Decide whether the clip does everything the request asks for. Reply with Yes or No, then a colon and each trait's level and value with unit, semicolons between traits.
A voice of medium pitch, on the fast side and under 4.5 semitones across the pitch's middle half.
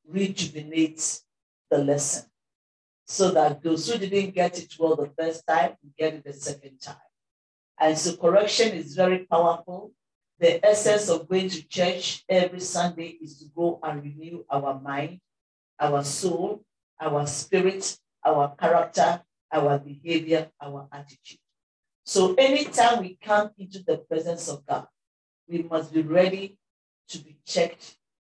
No: medium, 165 Hz; average, 140 wpm; average, 3.7 semitones